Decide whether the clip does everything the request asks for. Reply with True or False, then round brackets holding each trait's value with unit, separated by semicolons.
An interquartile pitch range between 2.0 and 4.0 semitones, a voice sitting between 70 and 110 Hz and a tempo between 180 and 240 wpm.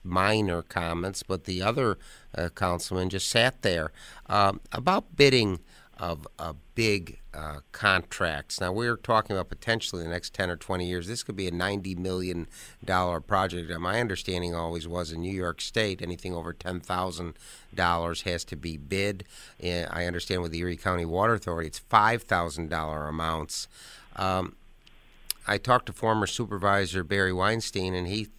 False (2.8 semitones; 90 Hz; 160 wpm)